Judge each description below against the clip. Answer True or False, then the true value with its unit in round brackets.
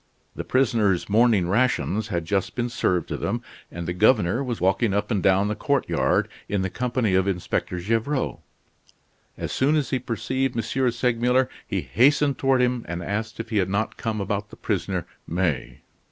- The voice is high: False (110 Hz)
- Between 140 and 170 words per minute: False (180 wpm)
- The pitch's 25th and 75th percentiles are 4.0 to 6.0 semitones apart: True (4.6 semitones)